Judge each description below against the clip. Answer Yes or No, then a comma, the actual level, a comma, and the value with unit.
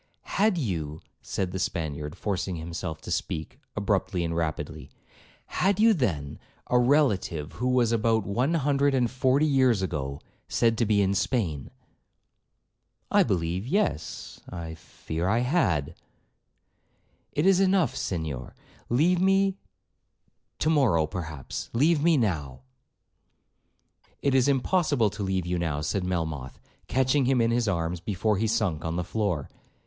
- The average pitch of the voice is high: No, low, 105 Hz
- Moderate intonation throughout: No, wide, 8.1 semitones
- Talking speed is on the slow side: Yes, slow, 130 wpm